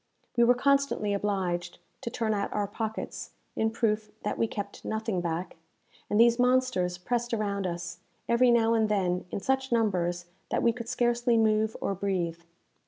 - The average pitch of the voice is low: No, high, 215 Hz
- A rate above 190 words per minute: No, average, 170 wpm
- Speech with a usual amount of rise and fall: Yes, average, 4.0 semitones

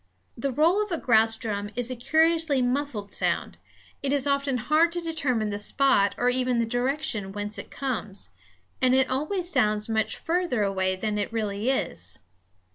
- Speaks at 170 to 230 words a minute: Yes, average, 175 wpm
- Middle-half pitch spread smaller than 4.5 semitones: No, average, 5.3 semitones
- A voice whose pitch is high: Yes, very high, 250 Hz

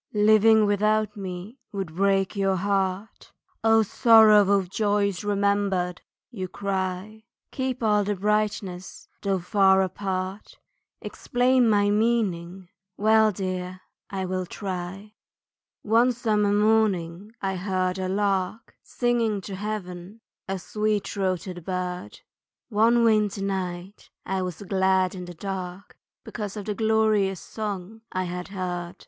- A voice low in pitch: No, high, 200 Hz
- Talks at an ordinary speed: No, slow, 125 wpm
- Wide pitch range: No, narrow, 2.5 semitones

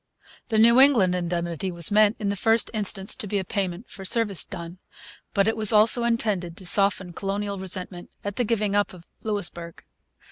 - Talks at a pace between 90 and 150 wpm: No, average, 185 wpm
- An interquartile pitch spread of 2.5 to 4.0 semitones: Yes, average, 3.0 semitones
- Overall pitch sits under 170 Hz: No, high, 200 Hz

